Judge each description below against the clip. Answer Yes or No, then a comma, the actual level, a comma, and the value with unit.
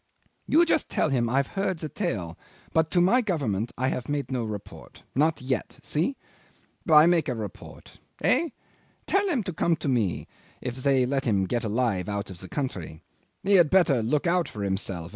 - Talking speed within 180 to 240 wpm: Yes, average, 190 wpm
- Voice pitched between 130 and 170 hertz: Yes, low, 135 Hz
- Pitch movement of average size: No, wide, 8.0 semitones